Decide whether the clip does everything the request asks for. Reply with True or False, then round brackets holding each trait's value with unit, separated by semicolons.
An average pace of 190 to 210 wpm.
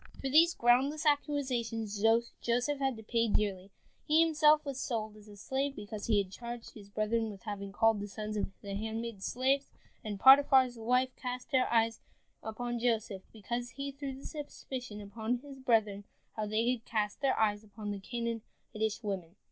False (175 wpm)